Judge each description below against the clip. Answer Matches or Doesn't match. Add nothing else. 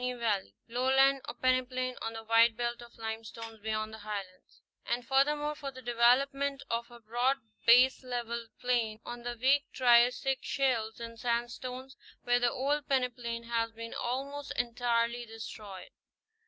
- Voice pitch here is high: Matches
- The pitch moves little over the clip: Matches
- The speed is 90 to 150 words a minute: Matches